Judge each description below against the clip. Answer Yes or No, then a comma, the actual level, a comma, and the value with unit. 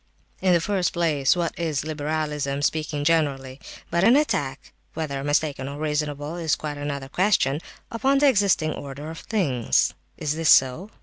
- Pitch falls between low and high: Yes, medium, 155 Hz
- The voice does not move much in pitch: No, average, 3.2 semitones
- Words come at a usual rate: Yes, average, 160 wpm